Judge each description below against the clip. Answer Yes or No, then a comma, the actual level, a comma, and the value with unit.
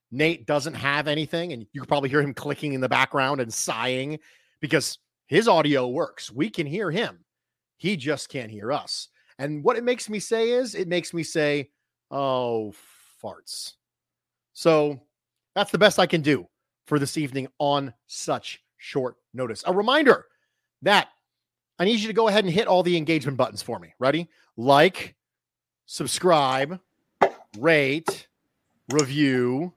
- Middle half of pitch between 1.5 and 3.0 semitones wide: No, average, 4.3 semitones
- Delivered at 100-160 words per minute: Yes, average, 155 wpm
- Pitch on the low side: No, medium, 145 Hz